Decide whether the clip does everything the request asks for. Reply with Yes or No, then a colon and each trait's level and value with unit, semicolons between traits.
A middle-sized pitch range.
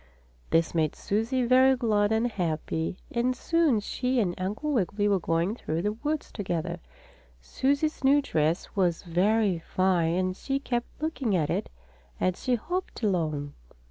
No: wide, 6.7 semitones